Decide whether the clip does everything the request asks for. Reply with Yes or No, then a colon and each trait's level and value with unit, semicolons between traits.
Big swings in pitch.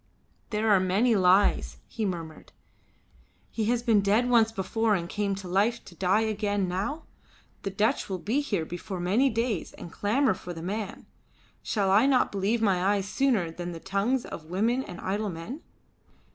No: average, 3.6 semitones